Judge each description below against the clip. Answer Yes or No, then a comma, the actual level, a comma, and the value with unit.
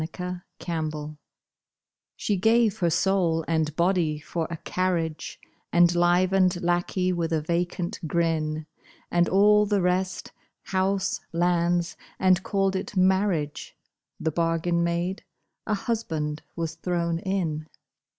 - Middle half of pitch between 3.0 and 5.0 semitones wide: No, narrow, 2.4 semitones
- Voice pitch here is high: No, medium, 175 Hz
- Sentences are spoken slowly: Yes, slow, 110 wpm